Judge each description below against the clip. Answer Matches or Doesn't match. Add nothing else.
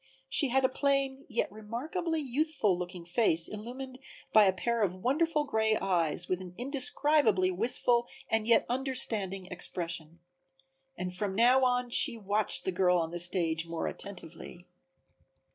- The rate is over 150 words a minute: Doesn't match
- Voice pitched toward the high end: Matches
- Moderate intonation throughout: Doesn't match